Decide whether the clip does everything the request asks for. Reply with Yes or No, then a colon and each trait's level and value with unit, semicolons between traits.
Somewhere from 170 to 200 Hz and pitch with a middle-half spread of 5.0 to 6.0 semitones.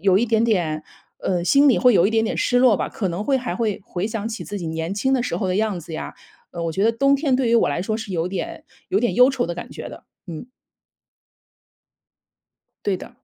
No: high, 215 Hz; average, 5.3 semitones